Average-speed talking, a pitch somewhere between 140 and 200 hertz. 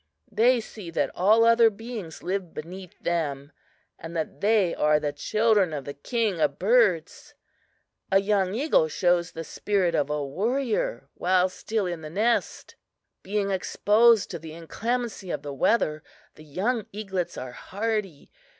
Yes: average, 150 wpm; high, 190 Hz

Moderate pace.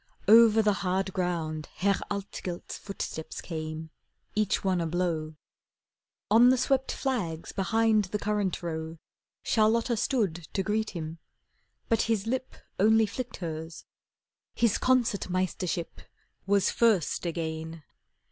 No: slow, 120 wpm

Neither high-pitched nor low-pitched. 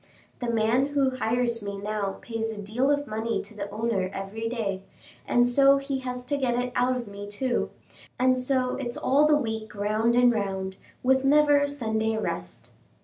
No: high, 235 Hz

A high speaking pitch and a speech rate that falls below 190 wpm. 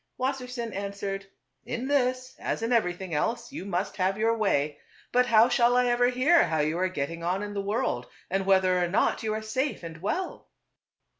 No: high, 210 Hz; fast, 205 wpm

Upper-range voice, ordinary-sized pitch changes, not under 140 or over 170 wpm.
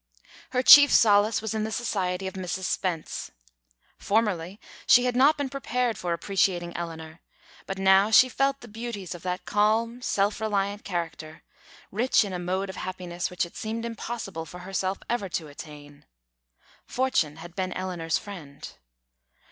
Yes: high, 195 Hz; average, 4.3 semitones; average, 155 wpm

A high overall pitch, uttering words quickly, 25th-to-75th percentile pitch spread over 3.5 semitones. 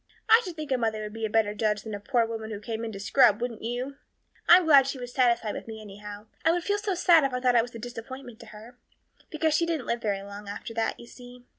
Yes: high, 235 Hz; fast, 275 wpm; average, 4.0 semitones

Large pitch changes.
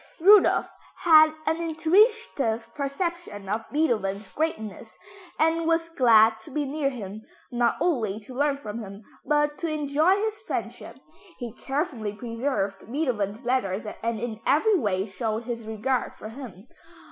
Yes: wide, 6.3 semitones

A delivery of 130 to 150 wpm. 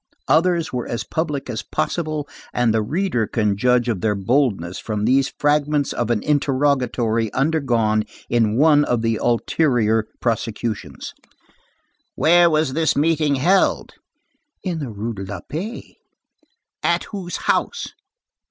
Yes: slow, 135 wpm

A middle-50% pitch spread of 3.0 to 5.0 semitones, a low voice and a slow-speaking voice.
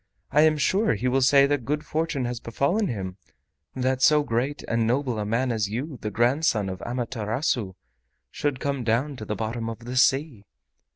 No: average, 4.0 semitones; low, 125 Hz; average, 185 wpm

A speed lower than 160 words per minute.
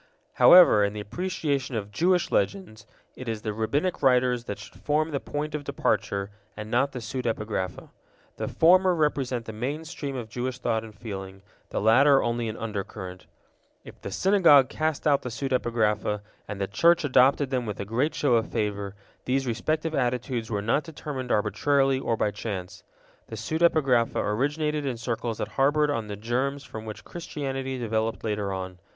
No: average, 170 wpm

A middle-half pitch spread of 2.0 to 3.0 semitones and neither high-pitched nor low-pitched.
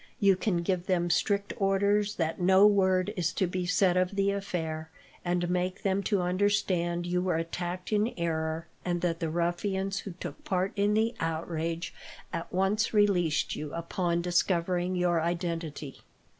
Yes: narrow, 2.4 semitones; medium, 180 Hz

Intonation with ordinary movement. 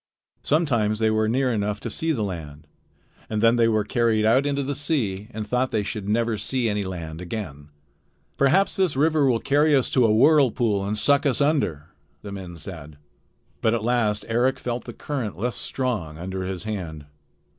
Yes: average, 4.7 semitones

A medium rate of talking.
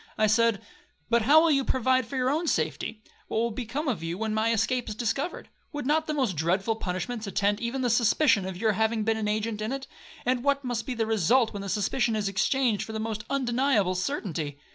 No: fast, 225 wpm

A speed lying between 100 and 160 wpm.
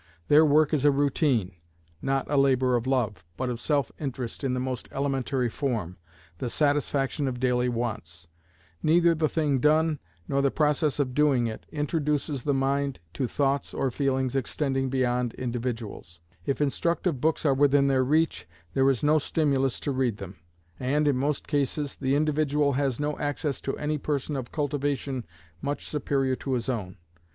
No: average, 170 wpm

